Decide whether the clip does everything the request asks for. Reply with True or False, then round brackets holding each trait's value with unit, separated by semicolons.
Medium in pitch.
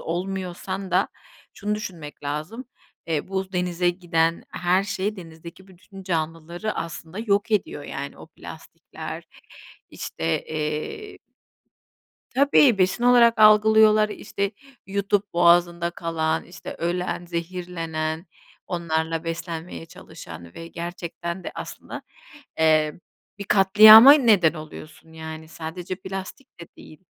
True (175 Hz)